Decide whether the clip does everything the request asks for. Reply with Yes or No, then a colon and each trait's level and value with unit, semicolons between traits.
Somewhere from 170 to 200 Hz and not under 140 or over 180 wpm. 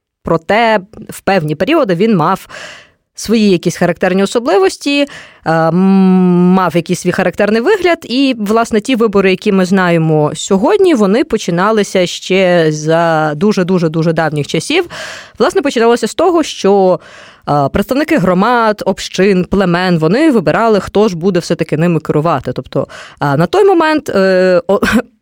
No: high, 190 Hz; average, 125 wpm